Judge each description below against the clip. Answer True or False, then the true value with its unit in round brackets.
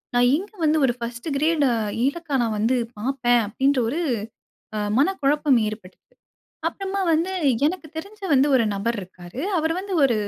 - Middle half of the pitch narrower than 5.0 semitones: False (5.4 semitones)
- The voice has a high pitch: True (275 Hz)